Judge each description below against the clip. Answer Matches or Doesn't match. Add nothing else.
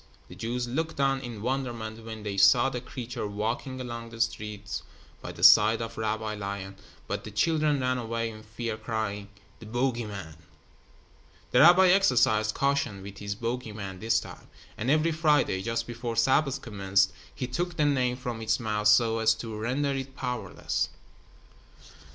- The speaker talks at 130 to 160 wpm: Doesn't match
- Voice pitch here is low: Matches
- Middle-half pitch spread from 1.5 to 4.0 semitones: Matches